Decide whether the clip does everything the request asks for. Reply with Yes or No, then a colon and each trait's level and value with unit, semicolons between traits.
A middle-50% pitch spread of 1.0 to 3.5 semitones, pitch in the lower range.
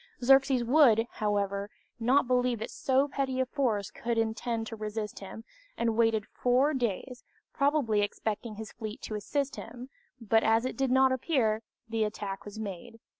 No: average, 3.2 semitones; high, 230 Hz